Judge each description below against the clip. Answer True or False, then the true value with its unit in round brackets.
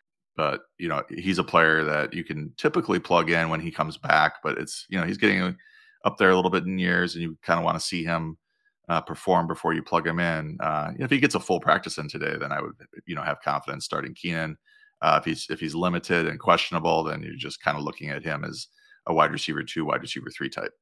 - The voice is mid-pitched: False (85 Hz)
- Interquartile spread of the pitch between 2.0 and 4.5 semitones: True (2.8 semitones)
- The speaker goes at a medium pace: False (255 wpm)